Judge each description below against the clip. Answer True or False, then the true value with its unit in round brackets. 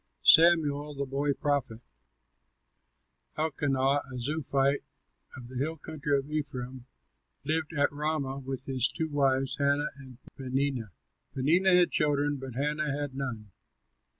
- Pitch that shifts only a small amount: True (2.0 semitones)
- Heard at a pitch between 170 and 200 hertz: False (140 Hz)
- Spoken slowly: True (125 wpm)